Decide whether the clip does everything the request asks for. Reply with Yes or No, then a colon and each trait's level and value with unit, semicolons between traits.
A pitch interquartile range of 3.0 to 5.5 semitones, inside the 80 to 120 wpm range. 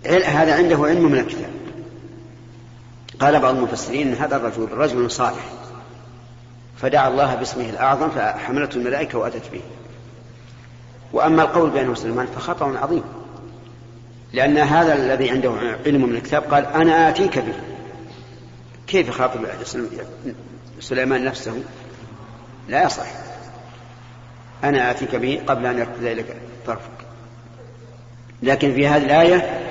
No: narrow, 2.4 semitones; average, 115 wpm